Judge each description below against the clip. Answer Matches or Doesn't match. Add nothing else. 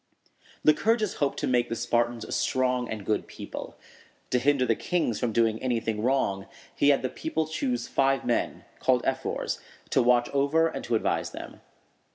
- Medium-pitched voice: Doesn't match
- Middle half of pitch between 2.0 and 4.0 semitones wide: Matches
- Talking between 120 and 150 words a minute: Doesn't match